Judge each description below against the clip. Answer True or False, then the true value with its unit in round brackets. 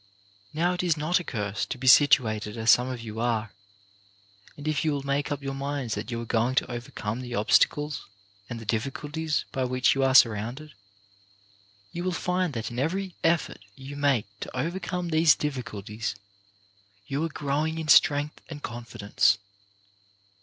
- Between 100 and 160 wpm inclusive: False (170 wpm)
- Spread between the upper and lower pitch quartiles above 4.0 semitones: True (4.7 semitones)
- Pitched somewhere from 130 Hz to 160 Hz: True (135 Hz)